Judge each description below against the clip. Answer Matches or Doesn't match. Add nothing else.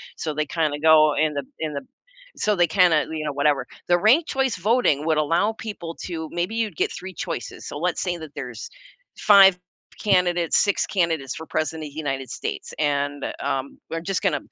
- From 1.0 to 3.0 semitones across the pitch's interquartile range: Doesn't match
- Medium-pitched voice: Matches